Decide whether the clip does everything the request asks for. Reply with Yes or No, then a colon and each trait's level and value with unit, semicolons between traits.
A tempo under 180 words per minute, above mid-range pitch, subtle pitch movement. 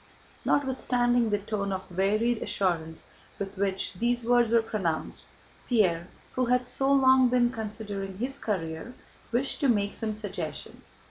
No: average, 140 wpm; high, 220 Hz; average, 4.0 semitones